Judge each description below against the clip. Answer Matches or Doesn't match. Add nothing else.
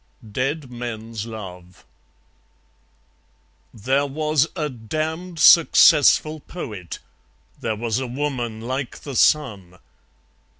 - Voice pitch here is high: Doesn't match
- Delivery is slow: Matches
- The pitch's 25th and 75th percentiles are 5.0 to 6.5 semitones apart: Matches